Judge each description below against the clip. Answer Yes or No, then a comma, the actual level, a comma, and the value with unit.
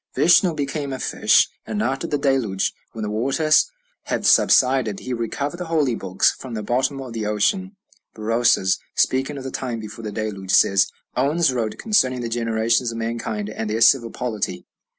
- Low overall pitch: Yes, low, 120 Hz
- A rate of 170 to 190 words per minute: Yes, average, 175 wpm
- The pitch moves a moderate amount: Yes, average, 4.0 semitones